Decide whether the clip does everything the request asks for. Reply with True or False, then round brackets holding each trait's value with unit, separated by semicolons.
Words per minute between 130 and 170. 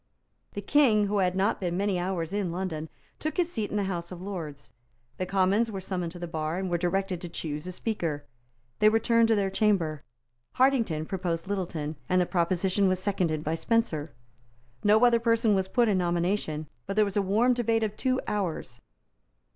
False (195 wpm)